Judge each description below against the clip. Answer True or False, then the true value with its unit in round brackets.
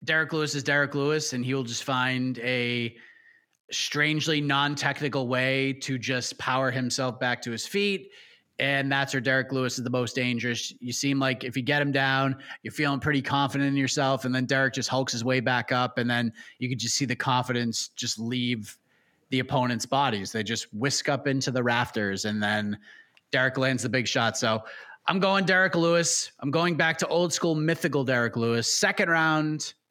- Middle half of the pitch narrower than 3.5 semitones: True (2.8 semitones)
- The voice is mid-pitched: False (130 Hz)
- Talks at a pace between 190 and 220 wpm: True (195 wpm)